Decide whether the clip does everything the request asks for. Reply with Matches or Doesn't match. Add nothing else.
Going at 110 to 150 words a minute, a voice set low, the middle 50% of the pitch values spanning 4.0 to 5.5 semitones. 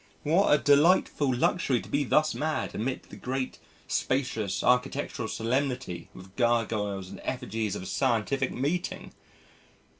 Matches